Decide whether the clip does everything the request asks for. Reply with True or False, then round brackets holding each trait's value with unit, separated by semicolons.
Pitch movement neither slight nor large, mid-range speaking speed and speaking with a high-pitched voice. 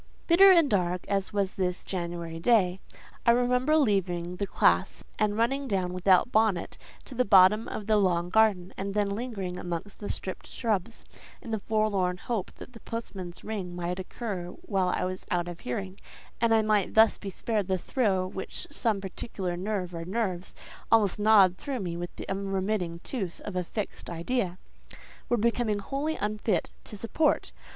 True (3.6 semitones; 170 wpm; 200 Hz)